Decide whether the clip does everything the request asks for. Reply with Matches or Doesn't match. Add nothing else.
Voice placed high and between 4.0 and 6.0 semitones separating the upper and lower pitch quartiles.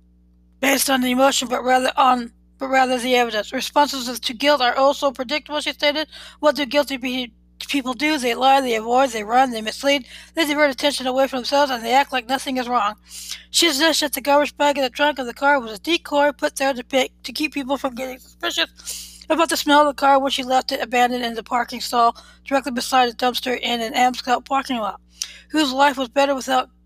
Doesn't match